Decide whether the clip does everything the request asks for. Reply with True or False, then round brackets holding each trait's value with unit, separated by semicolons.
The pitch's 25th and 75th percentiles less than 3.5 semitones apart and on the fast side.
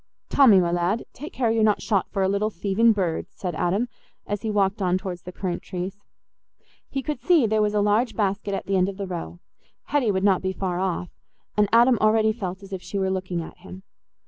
True (2.7 semitones; 225 wpm)